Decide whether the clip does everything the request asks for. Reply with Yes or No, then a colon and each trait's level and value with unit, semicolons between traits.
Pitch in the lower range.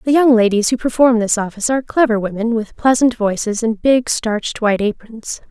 No: high, 230 Hz